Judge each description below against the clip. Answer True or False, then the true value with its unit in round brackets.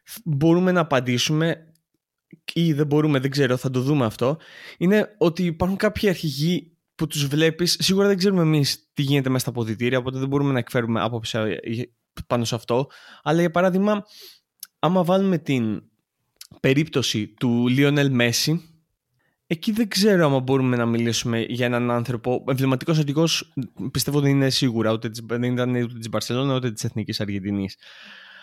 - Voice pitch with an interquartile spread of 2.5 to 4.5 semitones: False (5.3 semitones)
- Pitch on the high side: False (135 Hz)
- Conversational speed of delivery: True (150 wpm)